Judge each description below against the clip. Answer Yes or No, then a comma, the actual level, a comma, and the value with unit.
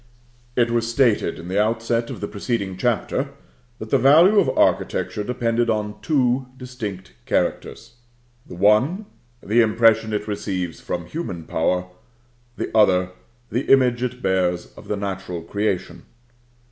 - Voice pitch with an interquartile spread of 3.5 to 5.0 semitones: Yes, average, 4.3 semitones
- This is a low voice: Yes, low, 110 Hz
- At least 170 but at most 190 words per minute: No, average, 140 wpm